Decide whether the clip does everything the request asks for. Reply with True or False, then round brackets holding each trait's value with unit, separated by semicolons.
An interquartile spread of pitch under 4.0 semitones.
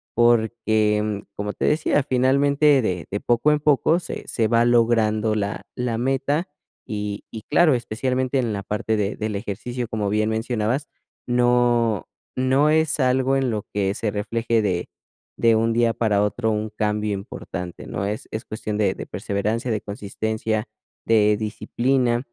True (2.9 semitones)